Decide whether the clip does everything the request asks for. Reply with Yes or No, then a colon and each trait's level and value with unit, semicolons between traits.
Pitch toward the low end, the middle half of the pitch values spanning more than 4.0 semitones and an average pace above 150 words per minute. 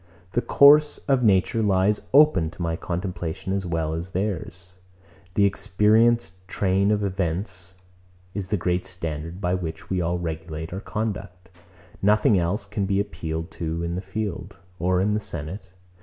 No: very low, 95 Hz; average, 3.2 semitones; average, 160 wpm